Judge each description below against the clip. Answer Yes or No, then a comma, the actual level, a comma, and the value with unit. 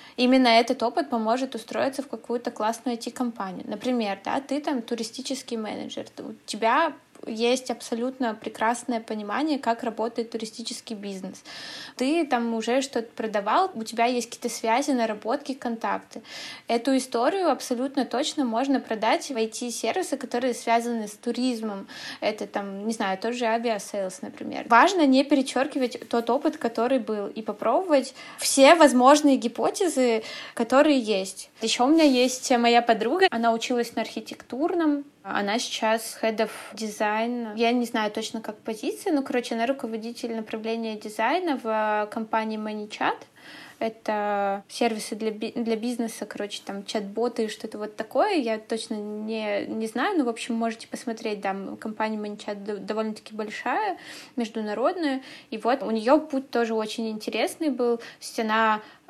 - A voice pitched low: No, high, 235 Hz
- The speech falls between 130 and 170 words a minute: Yes, average, 145 wpm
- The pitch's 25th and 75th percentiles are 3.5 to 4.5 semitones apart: No, average, 2.9 semitones